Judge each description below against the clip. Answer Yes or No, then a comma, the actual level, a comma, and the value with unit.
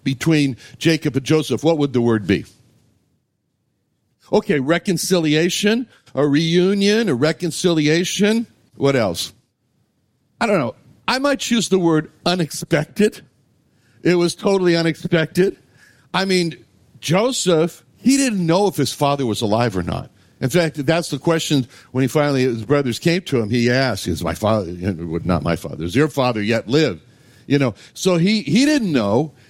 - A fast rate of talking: No, average, 155 wpm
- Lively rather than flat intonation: Yes, wide, 6.0 semitones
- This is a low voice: No, medium, 155 Hz